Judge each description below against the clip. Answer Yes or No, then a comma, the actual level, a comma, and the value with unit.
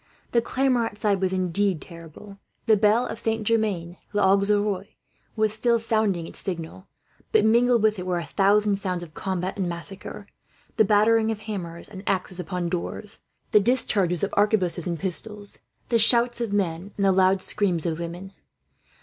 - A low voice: No, high, 200 Hz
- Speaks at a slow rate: No, average, 165 wpm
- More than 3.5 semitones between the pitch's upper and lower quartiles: No, average, 3.1 semitones